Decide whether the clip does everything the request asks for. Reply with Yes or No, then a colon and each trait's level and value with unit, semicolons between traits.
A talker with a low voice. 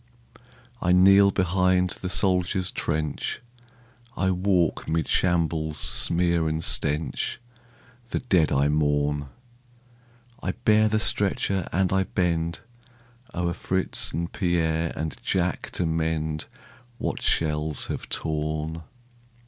Yes: very low, 85 Hz